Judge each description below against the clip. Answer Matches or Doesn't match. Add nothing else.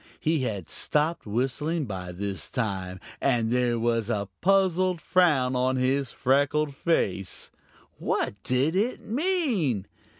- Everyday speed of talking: Doesn't match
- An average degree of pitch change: Doesn't match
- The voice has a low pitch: Matches